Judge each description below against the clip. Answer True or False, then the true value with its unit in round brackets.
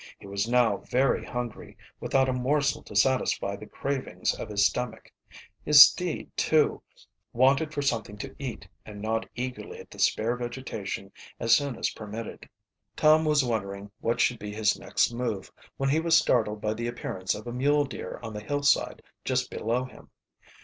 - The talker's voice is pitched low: True (120 Hz)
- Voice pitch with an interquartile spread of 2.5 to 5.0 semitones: True (4.3 semitones)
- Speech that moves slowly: False (175 wpm)